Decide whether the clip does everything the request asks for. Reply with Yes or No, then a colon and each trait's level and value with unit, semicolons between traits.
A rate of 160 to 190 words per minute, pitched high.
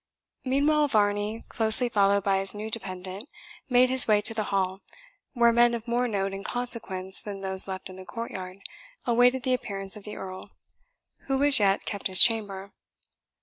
Yes: average, 175 wpm; high, 210 Hz